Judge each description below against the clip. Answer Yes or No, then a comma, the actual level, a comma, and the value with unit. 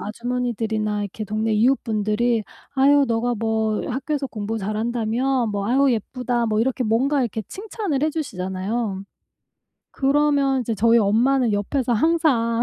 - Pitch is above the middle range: Yes, high, 235 Hz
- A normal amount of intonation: Yes, average, 3.8 semitones